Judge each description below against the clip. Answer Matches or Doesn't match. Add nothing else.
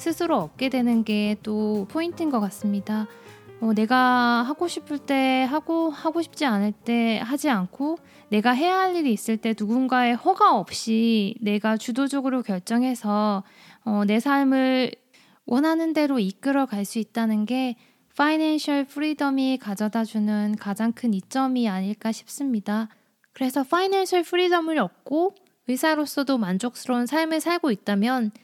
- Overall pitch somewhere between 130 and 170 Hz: Doesn't match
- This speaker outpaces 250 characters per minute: Matches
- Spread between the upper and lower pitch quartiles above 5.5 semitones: Doesn't match